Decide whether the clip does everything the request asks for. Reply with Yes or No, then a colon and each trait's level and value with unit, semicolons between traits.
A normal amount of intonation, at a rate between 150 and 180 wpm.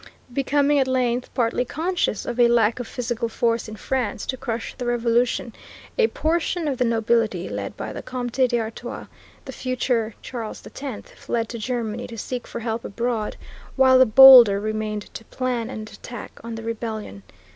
No: narrow, 2.2 semitones; average, 170 wpm